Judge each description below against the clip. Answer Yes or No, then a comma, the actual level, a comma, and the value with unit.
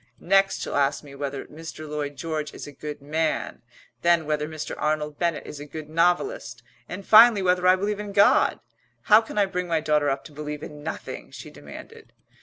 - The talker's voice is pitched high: No, medium, 155 Hz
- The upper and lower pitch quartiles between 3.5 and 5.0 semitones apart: Yes, average, 3.8 semitones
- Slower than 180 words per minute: No, average, 200 wpm